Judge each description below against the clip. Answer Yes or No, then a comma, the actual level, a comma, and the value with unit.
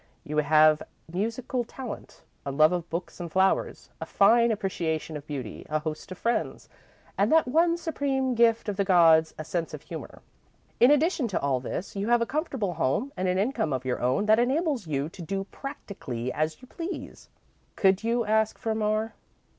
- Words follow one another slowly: No, average, 185 wpm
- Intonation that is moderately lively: No, wide, 7.2 semitones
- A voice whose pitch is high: Yes, high, 200 Hz